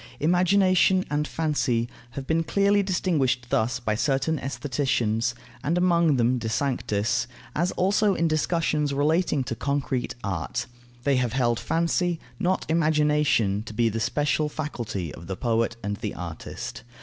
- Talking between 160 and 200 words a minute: No, average, 145 wpm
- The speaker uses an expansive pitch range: Yes, wide, 5.9 semitones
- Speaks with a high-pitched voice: No, medium, 140 Hz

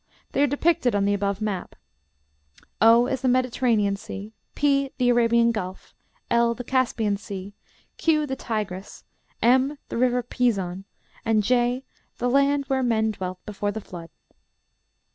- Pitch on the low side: No, high, 235 Hz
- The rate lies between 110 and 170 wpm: Yes, average, 145 wpm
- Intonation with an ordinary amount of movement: Yes, average, 3.9 semitones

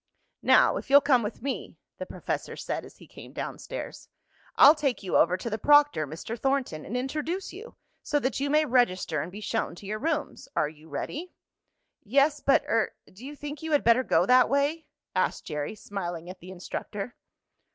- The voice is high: Yes, very high, 250 Hz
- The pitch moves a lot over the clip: Yes, wide, 7.5 semitones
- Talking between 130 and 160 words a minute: No, average, 195 wpm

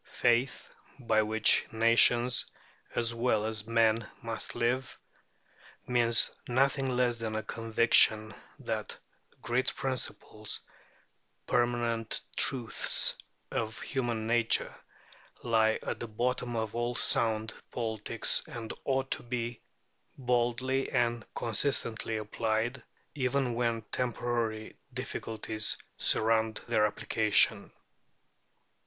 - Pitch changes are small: Yes, narrow, 1.8 semitones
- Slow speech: Yes, slow, 100 wpm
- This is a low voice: Yes, low, 115 Hz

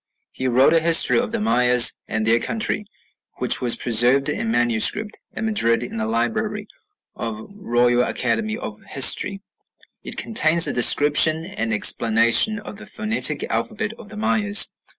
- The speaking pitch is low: No, medium, 155 Hz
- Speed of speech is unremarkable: Yes, average, 155 wpm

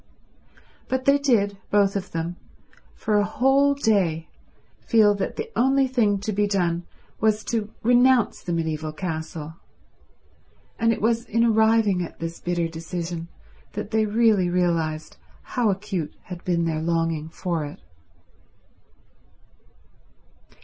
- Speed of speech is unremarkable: No, slow, 130 wpm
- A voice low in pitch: No, high, 200 Hz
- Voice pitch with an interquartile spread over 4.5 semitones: Yes, average, 5.2 semitones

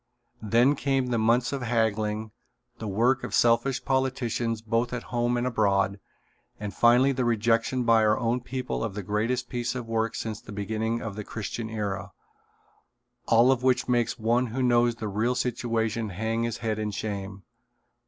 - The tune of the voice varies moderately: No, narrow, 2.1 semitones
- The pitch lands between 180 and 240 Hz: No, low, 115 Hz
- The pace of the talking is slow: No, average, 175 wpm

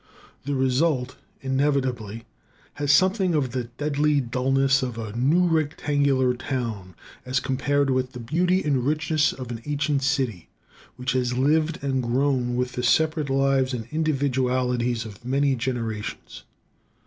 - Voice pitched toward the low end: Yes, low, 130 Hz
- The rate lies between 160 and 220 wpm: No, slow, 135 wpm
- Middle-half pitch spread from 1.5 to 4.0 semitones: Yes, narrow, 2.6 semitones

